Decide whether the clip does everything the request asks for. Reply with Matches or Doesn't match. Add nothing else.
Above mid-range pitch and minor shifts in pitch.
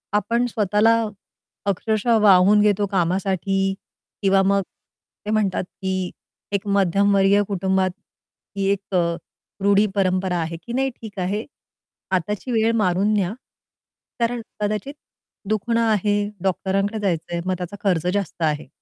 Matches